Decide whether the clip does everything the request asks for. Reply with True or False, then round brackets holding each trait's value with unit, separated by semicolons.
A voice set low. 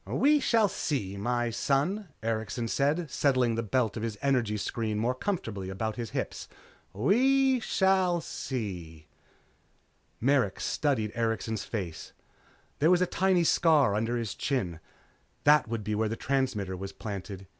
True (120 Hz)